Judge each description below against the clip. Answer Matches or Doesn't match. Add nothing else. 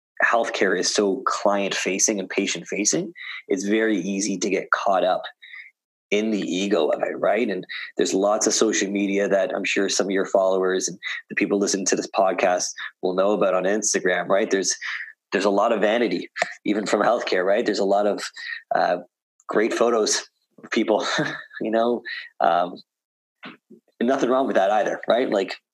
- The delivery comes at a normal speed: Matches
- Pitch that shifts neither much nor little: Doesn't match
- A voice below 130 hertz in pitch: Matches